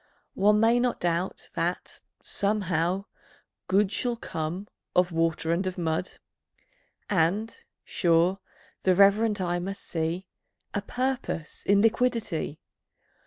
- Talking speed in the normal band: No, slow, 115 wpm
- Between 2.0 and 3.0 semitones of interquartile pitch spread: No, average, 3.8 semitones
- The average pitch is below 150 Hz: No, high, 190 Hz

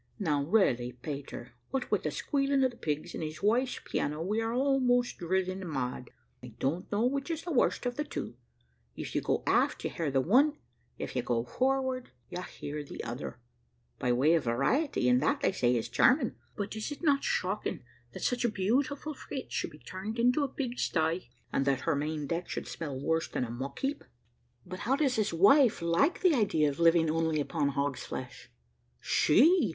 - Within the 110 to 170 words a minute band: No, average, 200 wpm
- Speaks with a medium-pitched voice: Yes, medium, 180 Hz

